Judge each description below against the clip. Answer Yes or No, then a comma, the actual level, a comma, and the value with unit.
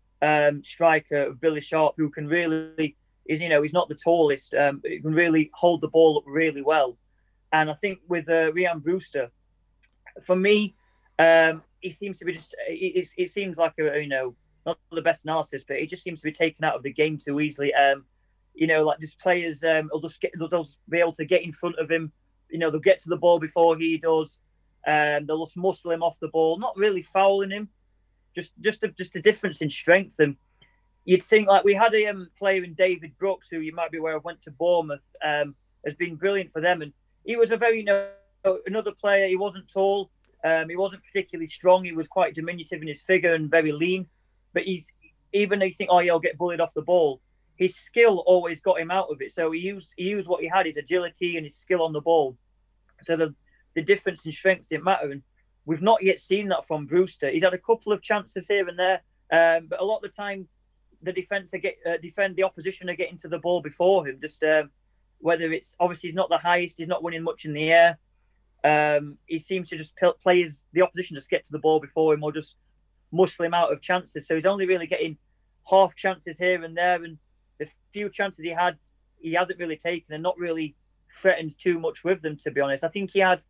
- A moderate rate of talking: No, fast, 230 wpm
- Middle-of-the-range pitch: Yes, medium, 170 Hz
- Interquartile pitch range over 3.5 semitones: No, average, 3.2 semitones